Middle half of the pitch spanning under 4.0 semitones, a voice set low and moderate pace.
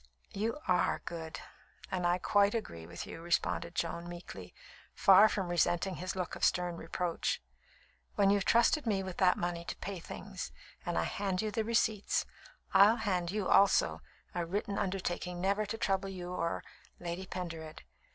No: narrow, 2.6 semitones; medium, 185 Hz; average, 165 wpm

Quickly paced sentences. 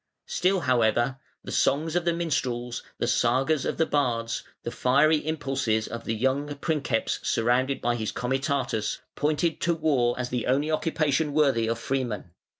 No: average, 155 wpm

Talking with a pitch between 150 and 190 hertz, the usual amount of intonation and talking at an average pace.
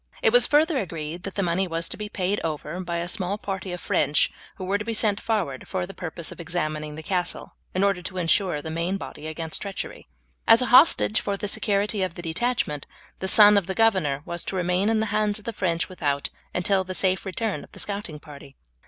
No: medium, 185 Hz; average, 3.6 semitones; fast, 230 wpm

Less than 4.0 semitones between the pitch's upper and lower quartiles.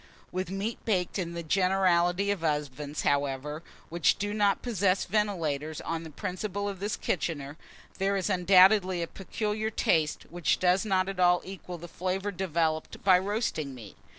Yes: average, 3.4 semitones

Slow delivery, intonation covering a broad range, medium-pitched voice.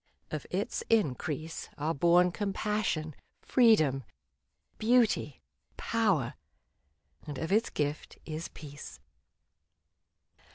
Yes: slow, 85 wpm; wide, 5.9 semitones; medium, 165 Hz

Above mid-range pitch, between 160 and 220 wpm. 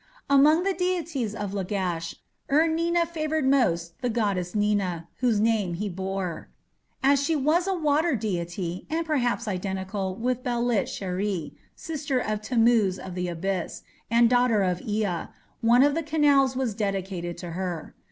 No: high, 220 Hz; average, 150 wpm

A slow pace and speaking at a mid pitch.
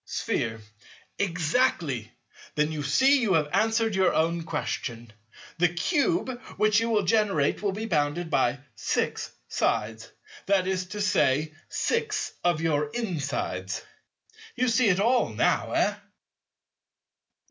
Yes: slow, 125 wpm; medium, 180 Hz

